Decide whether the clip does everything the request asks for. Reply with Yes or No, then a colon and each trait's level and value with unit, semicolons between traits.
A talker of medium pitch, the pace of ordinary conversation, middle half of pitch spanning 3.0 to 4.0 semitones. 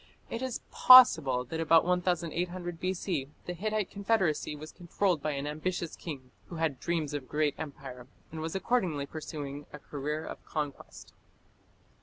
Yes: medium, 160 Hz; average, 155 wpm; average, 3.6 semitones